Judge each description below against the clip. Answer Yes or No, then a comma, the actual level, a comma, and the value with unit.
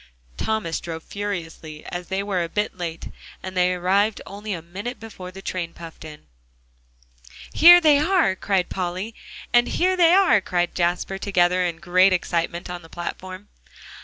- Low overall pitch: No, medium, 185 Hz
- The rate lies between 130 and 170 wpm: Yes, average, 160 wpm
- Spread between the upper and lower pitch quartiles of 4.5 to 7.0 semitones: No, average, 3.0 semitones